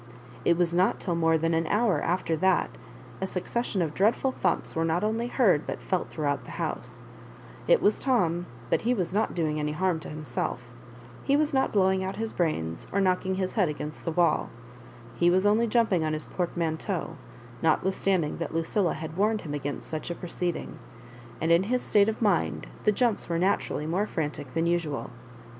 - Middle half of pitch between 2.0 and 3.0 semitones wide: No, average, 4.0 semitones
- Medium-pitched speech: Yes, medium, 175 Hz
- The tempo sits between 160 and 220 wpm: Yes, average, 195 wpm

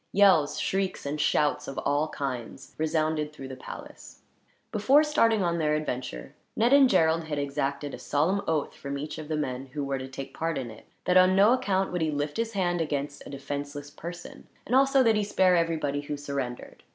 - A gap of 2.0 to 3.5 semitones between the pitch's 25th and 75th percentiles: No, average, 4.8 semitones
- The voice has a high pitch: No, medium, 155 Hz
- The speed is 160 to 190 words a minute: No, average, 200 wpm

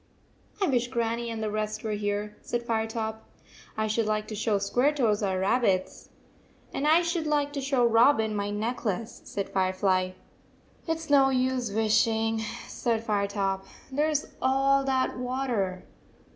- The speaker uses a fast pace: No, average, 170 wpm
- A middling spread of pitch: Yes, average, 4.0 semitones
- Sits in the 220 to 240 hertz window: Yes, high, 225 Hz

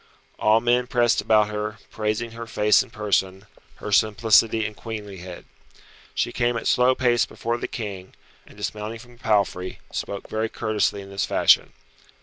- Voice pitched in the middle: No, low, 110 Hz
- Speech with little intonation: Yes, narrow, 2.2 semitones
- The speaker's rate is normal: Yes, average, 160 wpm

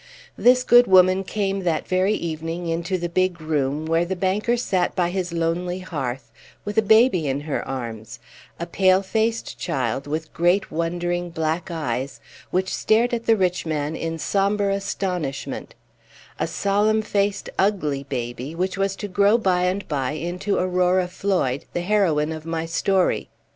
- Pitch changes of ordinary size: Yes, average, 3.6 semitones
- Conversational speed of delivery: Yes, average, 160 wpm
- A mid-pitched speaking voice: Yes, medium, 180 Hz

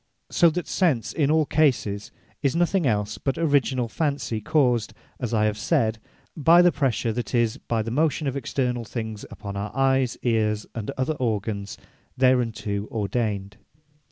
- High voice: No, low, 120 Hz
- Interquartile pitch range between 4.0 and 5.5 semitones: Yes, average, 4.6 semitones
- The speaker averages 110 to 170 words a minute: Yes, average, 155 wpm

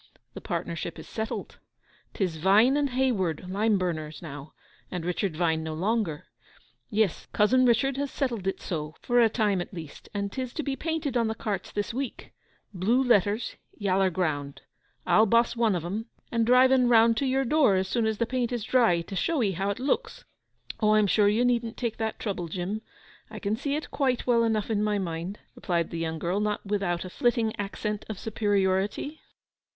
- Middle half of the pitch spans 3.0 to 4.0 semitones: No, average, 4.6 semitones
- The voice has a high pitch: Yes, high, 210 Hz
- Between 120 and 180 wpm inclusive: No, average, 190 wpm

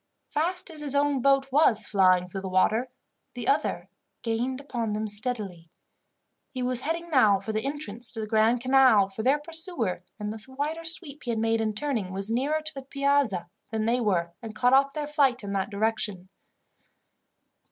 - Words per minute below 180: No, average, 185 wpm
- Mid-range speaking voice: No, high, 240 Hz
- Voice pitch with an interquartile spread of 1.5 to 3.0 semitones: No, average, 5.0 semitones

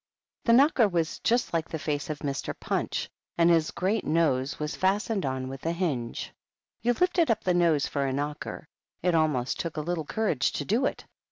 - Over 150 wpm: Yes, average, 195 wpm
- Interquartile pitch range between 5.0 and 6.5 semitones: Yes, wide, 5.4 semitones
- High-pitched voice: No, medium, 165 Hz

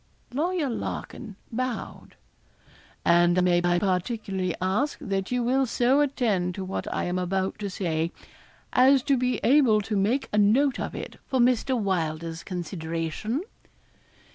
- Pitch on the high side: Yes, high, 205 Hz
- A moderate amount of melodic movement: No, wide, 5.9 semitones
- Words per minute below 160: Yes, average, 140 wpm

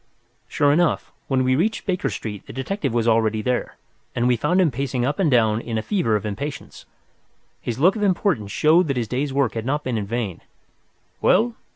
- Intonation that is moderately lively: No, wide, 5.7 semitones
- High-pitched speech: No, low, 130 Hz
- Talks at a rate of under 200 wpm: No, fast, 205 wpm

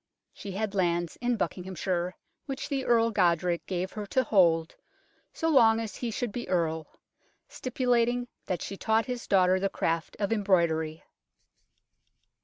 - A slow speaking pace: No, average, 145 wpm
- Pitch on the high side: Yes, high, 195 Hz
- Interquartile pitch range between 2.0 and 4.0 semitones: No, average, 4.9 semitones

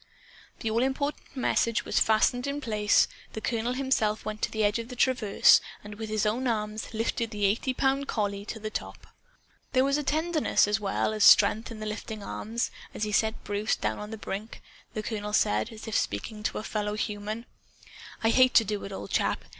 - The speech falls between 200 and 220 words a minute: Yes, fast, 205 wpm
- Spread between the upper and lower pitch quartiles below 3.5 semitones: Yes, narrow, 2.6 semitones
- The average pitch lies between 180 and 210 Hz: No, high, 220 Hz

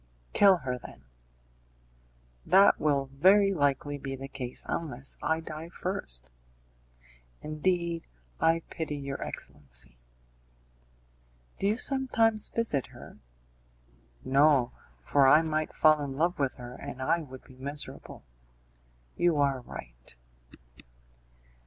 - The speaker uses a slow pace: Yes, slow, 115 wpm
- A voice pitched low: No, medium, 145 Hz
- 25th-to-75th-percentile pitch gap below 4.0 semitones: No, average, 4.3 semitones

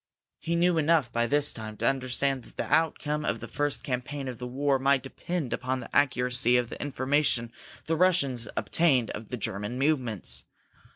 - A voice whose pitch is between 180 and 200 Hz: No, low, 135 Hz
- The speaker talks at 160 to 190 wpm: Yes, average, 180 wpm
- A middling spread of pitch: Yes, average, 3.1 semitones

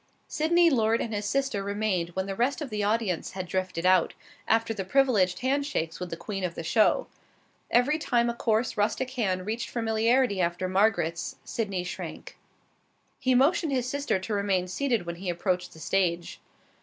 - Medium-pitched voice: No, high, 210 Hz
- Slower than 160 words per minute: No, average, 180 wpm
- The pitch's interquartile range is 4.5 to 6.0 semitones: Yes, average, 5.0 semitones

